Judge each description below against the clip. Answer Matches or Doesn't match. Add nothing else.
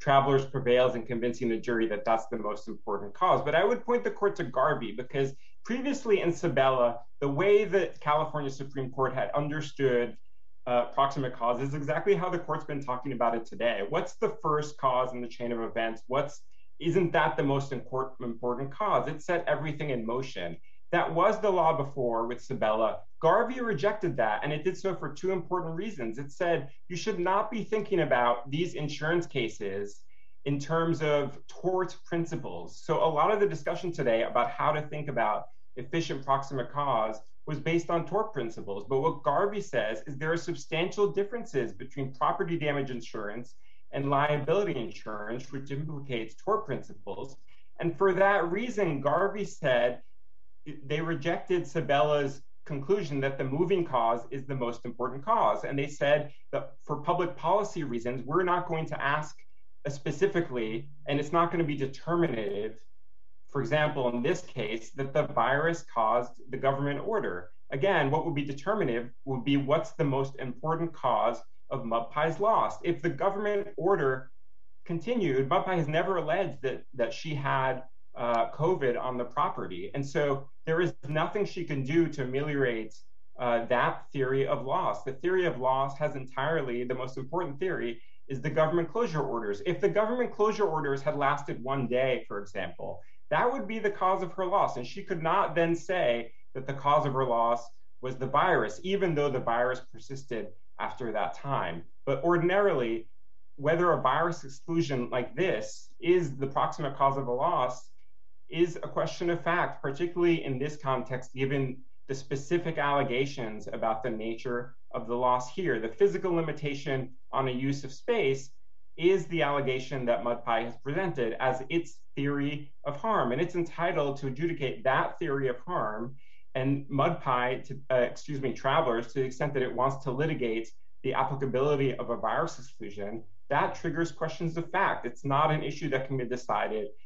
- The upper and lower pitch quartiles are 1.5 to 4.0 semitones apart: Doesn't match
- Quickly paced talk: Doesn't match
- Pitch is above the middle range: Doesn't match